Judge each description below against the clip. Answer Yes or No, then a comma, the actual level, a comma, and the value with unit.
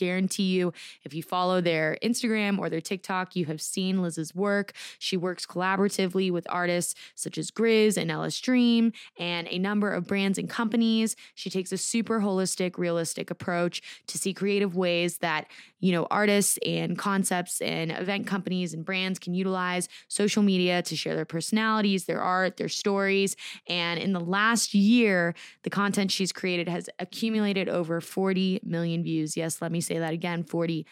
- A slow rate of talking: No, average, 175 wpm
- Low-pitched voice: No, medium, 185 Hz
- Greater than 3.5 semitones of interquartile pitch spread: No, average, 2.8 semitones